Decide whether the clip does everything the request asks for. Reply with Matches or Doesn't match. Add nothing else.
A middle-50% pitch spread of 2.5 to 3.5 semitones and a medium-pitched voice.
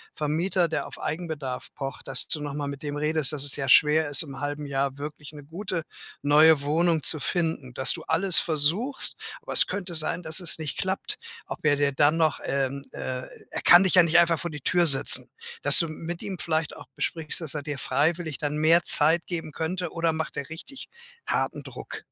Matches